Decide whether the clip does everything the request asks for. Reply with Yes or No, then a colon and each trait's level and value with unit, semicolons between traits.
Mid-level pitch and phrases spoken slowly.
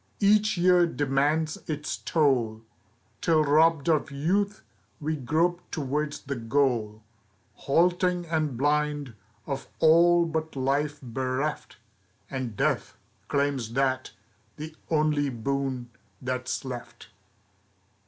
Yes: medium, 145 Hz; slow, 105 wpm